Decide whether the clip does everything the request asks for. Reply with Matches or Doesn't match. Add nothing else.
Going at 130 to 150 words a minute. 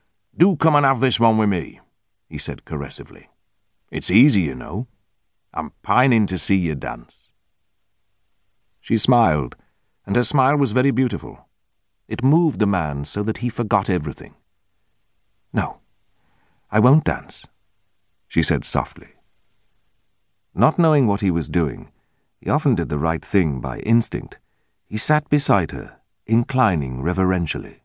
Matches